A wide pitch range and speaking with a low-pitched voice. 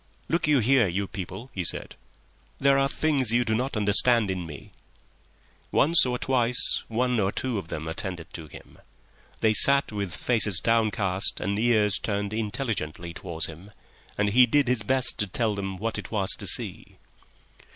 No: average, 4.4 semitones; low, 110 Hz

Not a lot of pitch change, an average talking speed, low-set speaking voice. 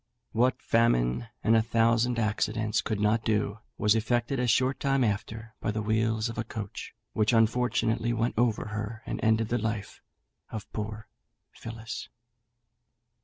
Yes: narrow, 1.5 semitones; average, 150 wpm; low, 110 Hz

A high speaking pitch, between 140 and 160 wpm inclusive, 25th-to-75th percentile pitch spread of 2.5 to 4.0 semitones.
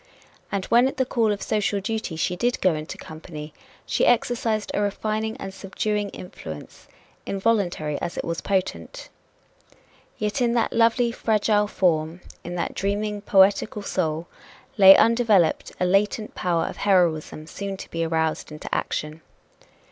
No: high, 195 Hz; average, 150 wpm; average, 4.5 semitones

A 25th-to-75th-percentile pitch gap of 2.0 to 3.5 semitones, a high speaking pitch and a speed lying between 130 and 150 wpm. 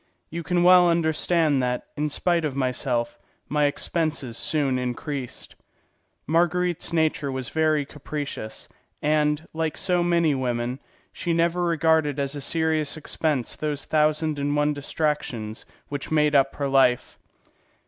No: average, 2.8 semitones; medium, 150 Hz; slow, 135 wpm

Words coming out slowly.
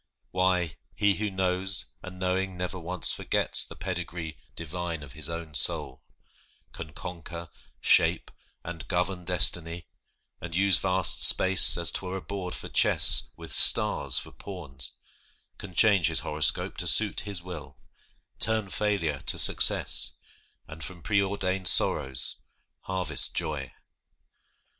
Yes: slow, 130 wpm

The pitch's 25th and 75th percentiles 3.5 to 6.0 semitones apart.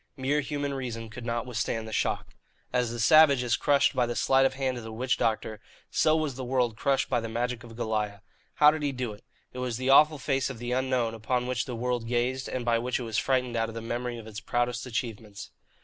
No: narrow, 2.4 semitones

